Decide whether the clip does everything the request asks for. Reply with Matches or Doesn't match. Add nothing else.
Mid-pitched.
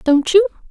Doesn't match